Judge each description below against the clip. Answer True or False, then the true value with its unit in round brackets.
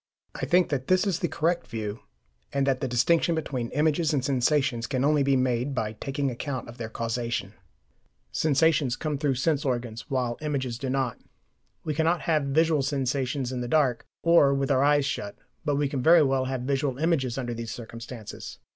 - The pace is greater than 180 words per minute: True (190 wpm)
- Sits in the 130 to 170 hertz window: True (135 Hz)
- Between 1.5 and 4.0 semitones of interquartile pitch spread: True (3.4 semitones)